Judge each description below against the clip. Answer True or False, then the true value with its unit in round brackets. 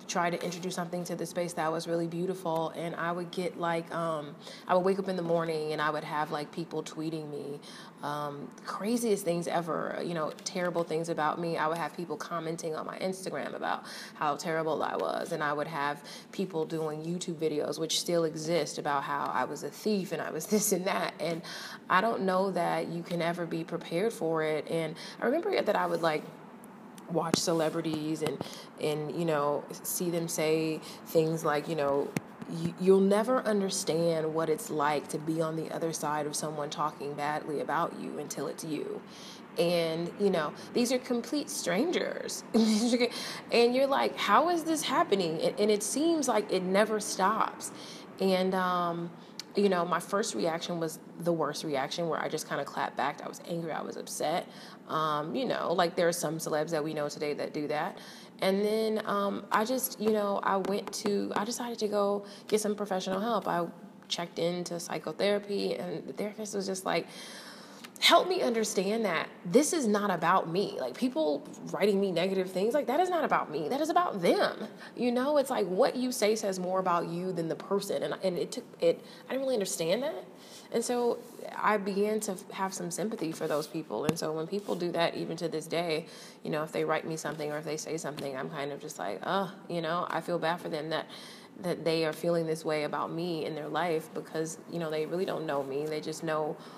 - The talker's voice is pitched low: False (175 Hz)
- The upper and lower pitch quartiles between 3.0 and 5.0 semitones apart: True (4.6 semitones)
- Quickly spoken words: True (210 wpm)